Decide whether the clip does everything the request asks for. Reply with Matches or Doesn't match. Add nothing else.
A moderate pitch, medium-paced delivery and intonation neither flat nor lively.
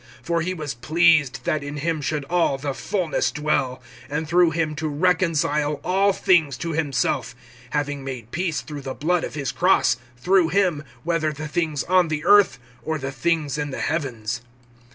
Matches